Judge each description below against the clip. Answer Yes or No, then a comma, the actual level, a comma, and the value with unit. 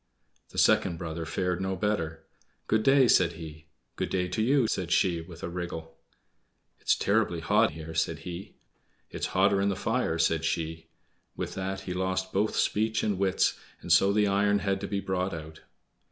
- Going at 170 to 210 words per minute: Yes, average, 180 wpm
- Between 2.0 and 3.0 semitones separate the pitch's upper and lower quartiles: No, average, 3.4 semitones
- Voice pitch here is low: Yes, very low, 95 Hz